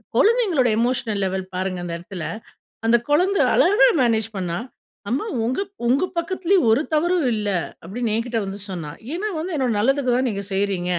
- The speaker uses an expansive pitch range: Yes, wide, 7.9 semitones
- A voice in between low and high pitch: No, high, 235 Hz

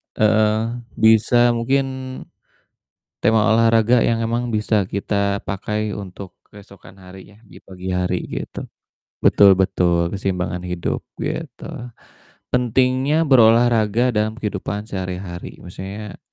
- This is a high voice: No, low, 105 Hz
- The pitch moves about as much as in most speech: Yes, average, 3.3 semitones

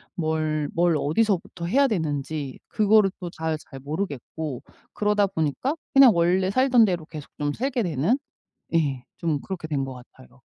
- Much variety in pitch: Yes, wide, 5.7 semitones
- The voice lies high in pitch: No, medium, 165 Hz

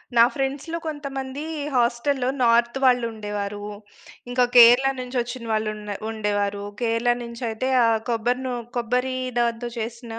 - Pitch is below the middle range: No, high, 240 Hz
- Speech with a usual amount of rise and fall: No, narrow, 2.2 semitones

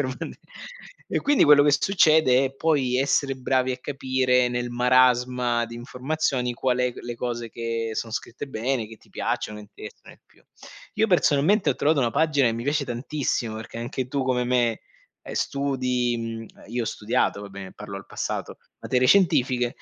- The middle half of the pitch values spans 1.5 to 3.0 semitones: Yes, average, 2.7 semitones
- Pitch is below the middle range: Yes, low, 125 Hz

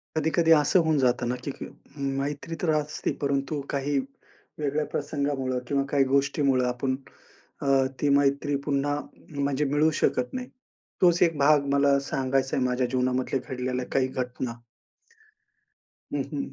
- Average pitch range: No, narrow, 2.1 semitones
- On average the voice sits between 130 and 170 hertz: Yes, medium, 140 Hz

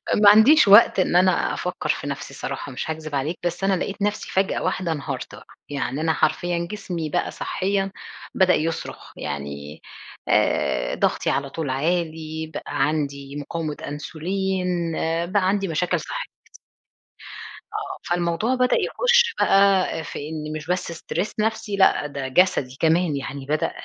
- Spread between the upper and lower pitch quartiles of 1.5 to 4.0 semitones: No, average, 4.6 semitones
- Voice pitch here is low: No, medium, 170 Hz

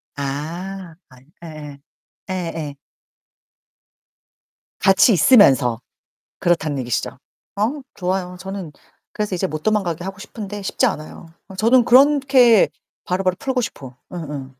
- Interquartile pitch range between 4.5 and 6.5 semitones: Yes, wide, 5.4 semitones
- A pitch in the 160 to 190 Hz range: Yes, medium, 185 Hz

